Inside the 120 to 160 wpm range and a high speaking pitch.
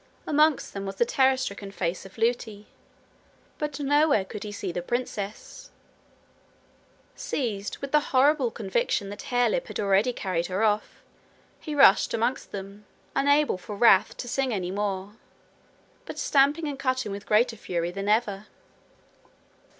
Yes: average, 145 wpm; high, 215 Hz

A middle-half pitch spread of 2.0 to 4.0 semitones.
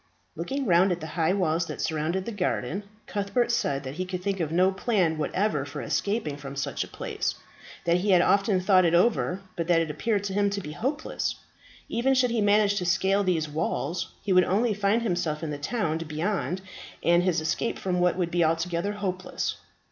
Yes: average, 3.6 semitones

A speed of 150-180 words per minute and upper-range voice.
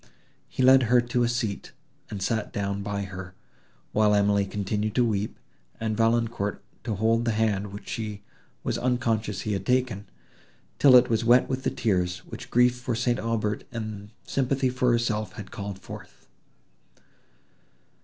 No: average, 160 wpm; low, 110 Hz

